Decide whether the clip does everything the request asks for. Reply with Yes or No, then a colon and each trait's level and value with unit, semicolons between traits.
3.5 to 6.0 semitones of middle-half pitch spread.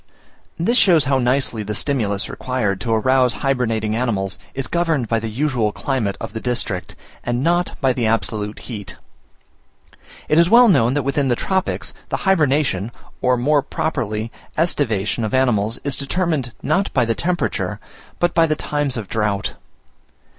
Yes: average, 5.1 semitones